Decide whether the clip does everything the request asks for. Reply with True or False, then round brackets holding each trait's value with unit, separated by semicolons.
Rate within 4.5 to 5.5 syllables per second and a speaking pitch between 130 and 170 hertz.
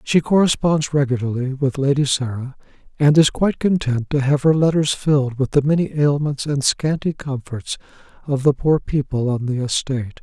True (5.2 syllables/s; 140 Hz)